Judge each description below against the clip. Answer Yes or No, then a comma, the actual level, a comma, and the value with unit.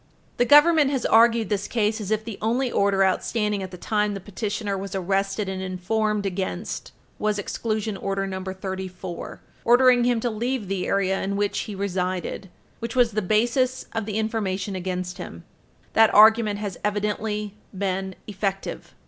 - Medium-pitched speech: No, high, 205 Hz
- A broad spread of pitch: No, narrow, 2.6 semitones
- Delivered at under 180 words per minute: Yes, average, 165 wpm